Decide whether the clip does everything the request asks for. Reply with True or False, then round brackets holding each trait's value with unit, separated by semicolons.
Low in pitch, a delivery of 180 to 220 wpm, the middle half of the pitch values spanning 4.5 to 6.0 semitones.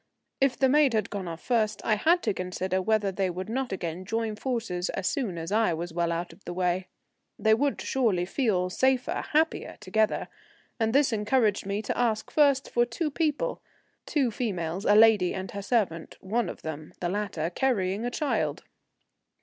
False (210 Hz; 185 wpm; 5.1 semitones)